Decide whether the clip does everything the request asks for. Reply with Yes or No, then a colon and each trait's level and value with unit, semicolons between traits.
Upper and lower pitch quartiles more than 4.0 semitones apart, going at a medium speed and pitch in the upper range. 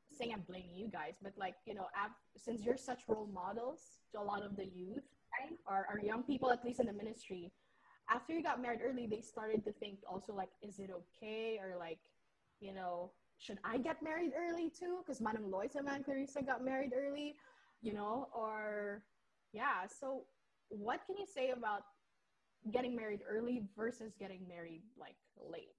Yes: average, 4.4 semitones; average, 190 wpm; high, 220 Hz